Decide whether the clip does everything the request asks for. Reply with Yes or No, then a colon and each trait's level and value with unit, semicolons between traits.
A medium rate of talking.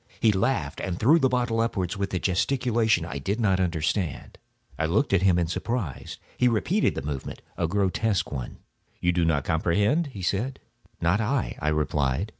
Yes: average, 175 wpm